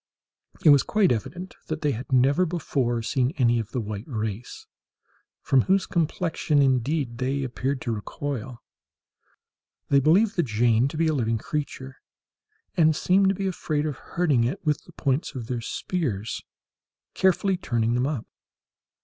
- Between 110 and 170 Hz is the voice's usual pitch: Yes, medium, 140 Hz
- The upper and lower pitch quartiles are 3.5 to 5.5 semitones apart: Yes, average, 5.1 semitones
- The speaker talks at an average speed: Yes, average, 155 wpm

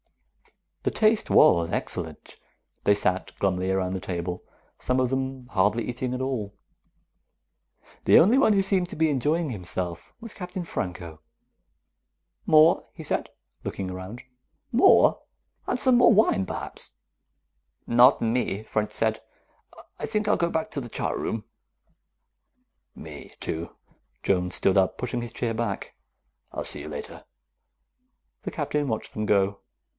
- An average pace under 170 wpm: Yes, average, 140 wpm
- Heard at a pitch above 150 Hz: No, low, 120 Hz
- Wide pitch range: Yes, wide, 8.6 semitones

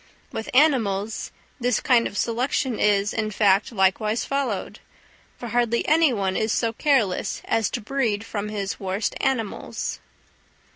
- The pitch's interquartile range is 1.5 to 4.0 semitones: Yes, average, 3.3 semitones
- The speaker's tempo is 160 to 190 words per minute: No, average, 140 wpm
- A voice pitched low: No, high, 225 Hz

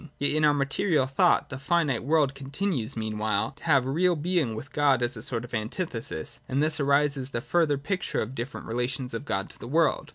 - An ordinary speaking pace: No, fast, 215 wpm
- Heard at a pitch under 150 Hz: Yes, low, 135 Hz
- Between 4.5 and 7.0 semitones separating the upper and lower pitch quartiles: No, average, 4.1 semitones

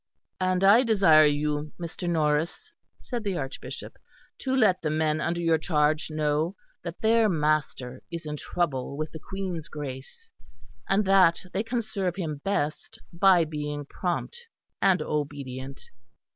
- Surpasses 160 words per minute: No, average, 145 wpm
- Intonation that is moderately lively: Yes, average, 4.4 semitones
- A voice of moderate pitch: Yes, medium, 165 Hz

